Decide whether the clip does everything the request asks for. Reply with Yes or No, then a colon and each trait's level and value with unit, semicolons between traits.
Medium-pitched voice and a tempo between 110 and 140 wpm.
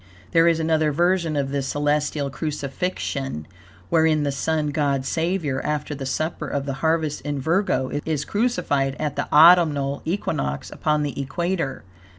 No: medium, 150 Hz; average, 150 wpm